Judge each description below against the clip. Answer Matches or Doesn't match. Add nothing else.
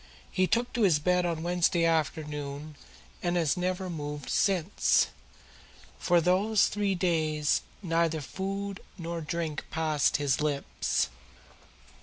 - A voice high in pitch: Doesn't match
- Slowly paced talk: Matches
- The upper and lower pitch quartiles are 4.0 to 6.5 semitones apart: Doesn't match